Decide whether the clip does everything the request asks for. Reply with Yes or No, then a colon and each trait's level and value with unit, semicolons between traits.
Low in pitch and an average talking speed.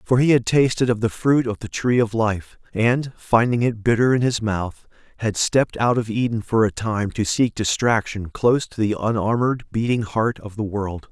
No: low, 115 Hz; fast, 210 wpm